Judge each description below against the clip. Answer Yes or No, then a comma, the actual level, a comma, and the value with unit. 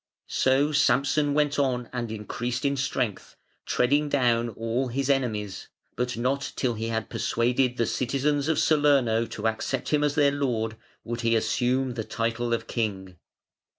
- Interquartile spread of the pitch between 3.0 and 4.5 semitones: Yes, average, 3.4 semitones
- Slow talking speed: No, average, 155 wpm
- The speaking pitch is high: No, low, 125 Hz